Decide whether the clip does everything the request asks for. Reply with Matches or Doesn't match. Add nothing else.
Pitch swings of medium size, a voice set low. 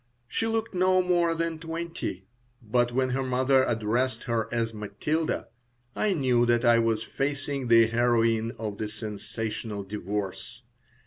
Matches